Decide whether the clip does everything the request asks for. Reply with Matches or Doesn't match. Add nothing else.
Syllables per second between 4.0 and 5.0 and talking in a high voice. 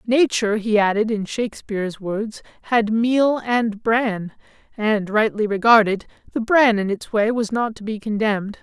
Matches